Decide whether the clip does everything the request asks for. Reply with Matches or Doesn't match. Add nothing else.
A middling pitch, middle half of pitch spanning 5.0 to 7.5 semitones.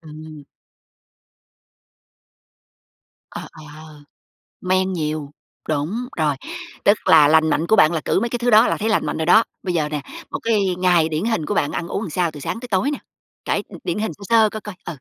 Matches